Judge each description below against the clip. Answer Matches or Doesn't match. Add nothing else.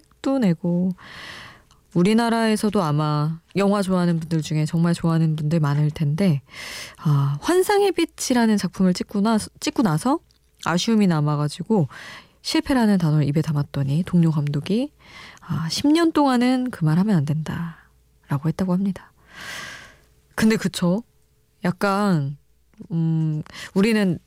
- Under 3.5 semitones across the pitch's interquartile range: Doesn't match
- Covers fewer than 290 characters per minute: Matches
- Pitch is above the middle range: Doesn't match